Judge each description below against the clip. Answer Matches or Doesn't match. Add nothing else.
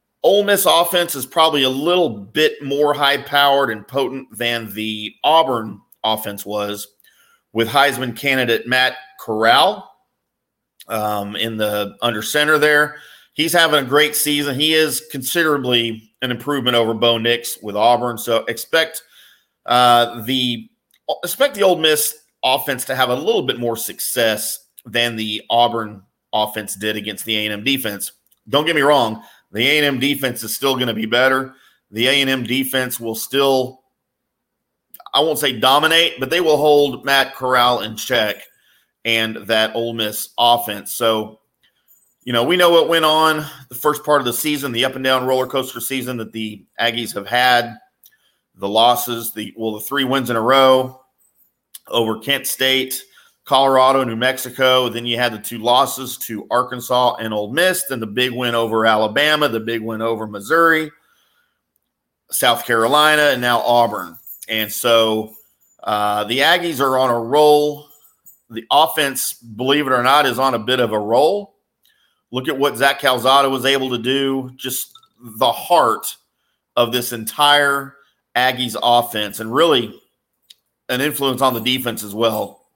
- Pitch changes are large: Doesn't match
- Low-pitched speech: Matches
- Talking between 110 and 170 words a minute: Matches